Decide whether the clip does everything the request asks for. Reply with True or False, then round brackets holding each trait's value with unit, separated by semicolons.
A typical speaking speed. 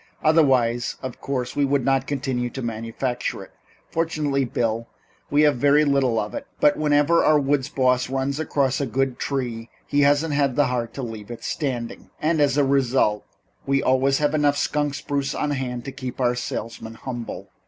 True (180 wpm)